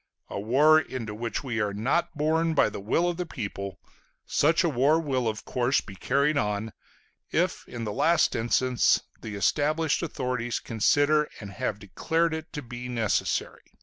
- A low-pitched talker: Yes, low, 125 Hz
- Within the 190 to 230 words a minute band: No, average, 170 wpm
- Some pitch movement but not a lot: No, wide, 5.9 semitones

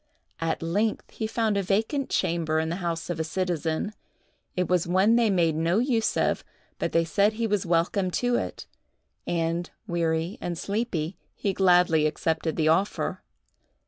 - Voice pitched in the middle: Yes, medium, 175 Hz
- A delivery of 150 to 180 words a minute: Yes, average, 165 wpm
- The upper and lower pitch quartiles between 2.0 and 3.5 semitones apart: No, average, 4.0 semitones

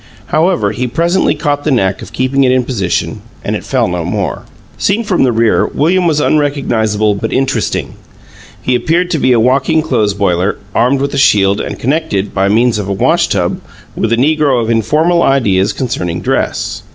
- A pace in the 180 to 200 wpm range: Yes, average, 190 wpm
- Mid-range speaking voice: No, low, 125 Hz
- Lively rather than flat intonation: Yes, wide, 6.1 semitones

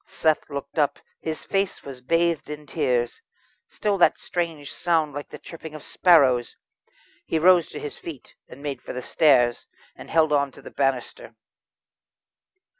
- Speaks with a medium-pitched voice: Yes, medium, 150 Hz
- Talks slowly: No, average, 160 wpm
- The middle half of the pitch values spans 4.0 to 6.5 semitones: No, average, 3.3 semitones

